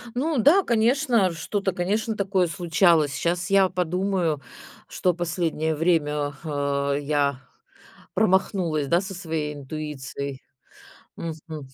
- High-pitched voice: No, medium, 170 Hz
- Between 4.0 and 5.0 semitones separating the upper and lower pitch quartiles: Yes, average, 4.4 semitones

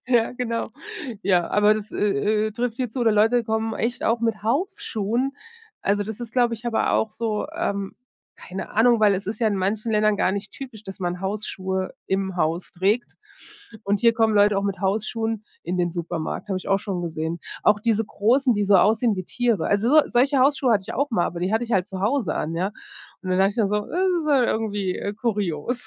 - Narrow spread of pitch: No, average, 3.3 semitones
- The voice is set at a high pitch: Yes, high, 215 Hz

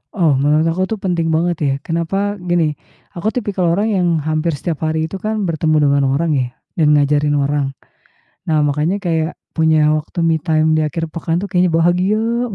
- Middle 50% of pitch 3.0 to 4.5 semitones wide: No, narrow, 2.4 semitones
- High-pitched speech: No, medium, 165 Hz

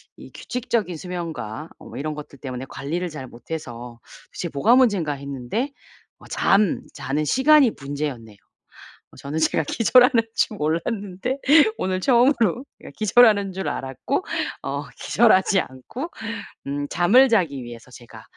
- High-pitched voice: No, medium, 165 Hz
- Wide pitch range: Yes, wide, 8.4 semitones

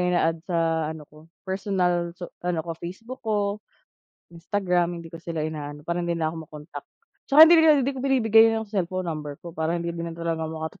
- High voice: No, medium, 170 Hz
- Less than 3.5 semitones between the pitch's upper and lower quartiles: No, average, 3.8 semitones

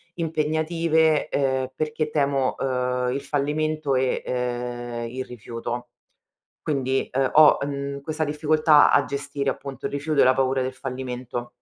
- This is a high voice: No, medium, 140 Hz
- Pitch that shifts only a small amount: No, average, 3.0 semitones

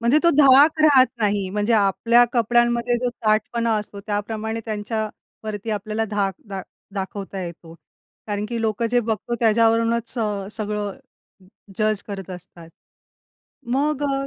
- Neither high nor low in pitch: No, high, 220 Hz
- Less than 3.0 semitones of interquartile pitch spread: Yes, narrow, 2.6 semitones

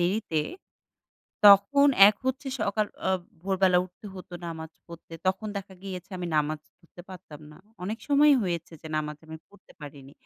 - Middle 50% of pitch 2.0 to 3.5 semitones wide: No, average, 4.0 semitones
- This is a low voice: No, medium, 185 Hz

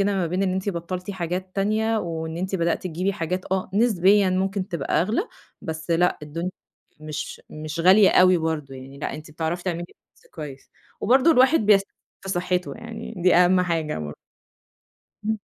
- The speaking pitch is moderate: Yes, medium, 180 Hz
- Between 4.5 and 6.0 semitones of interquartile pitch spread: No, average, 3.2 semitones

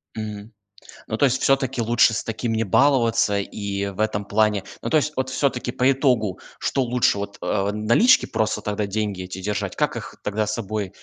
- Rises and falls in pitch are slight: No, average, 3.4 semitones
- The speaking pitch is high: No, low, 110 Hz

